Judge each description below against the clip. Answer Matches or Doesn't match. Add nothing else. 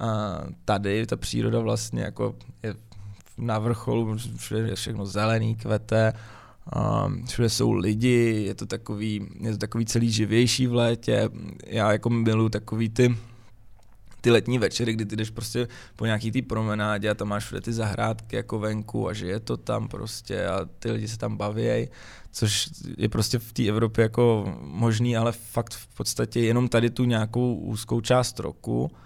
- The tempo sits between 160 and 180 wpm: Matches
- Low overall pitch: Matches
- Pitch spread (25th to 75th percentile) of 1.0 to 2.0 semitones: Matches